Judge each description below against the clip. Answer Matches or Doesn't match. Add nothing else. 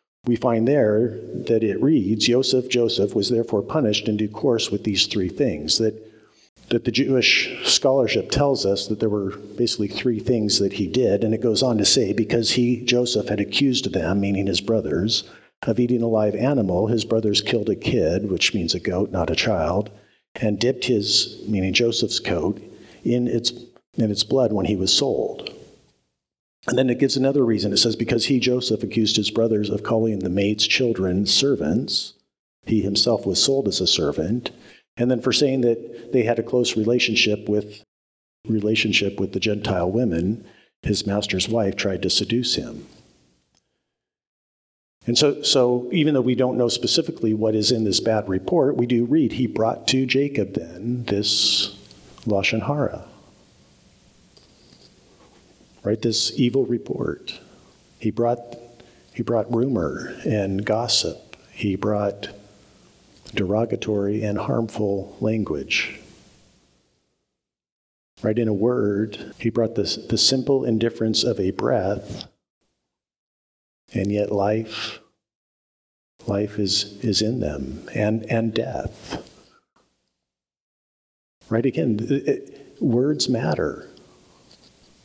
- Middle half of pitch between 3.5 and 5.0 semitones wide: Doesn't match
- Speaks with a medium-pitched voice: Doesn't match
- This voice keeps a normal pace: Matches